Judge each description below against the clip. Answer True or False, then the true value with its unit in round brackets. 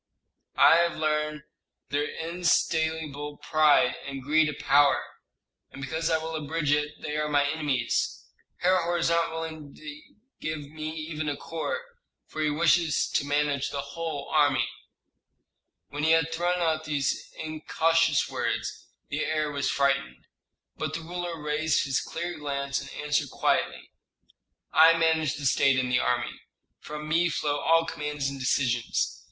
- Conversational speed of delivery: True (150 wpm)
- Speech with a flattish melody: True (2.2 semitones)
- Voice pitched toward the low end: False (150 Hz)